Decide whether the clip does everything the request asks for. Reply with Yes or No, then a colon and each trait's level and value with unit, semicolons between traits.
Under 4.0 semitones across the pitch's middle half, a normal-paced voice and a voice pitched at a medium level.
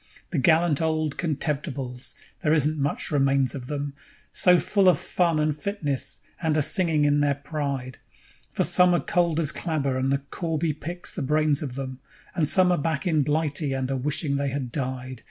Yes: average, 2.8 semitones; average, 190 wpm; medium, 150 Hz